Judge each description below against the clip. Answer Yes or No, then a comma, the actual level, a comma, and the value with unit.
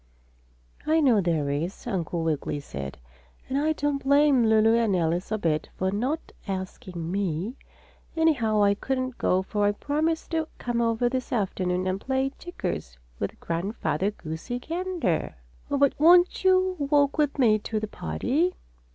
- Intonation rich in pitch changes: Yes, wide, 7.6 semitones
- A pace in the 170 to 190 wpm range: No, average, 155 wpm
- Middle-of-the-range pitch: No, high, 225 Hz